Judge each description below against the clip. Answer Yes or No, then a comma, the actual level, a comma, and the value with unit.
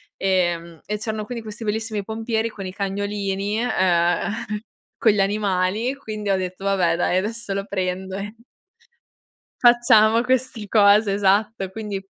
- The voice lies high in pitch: Yes, high, 205 Hz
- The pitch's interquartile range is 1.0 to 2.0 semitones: No, narrow, 2.5 semitones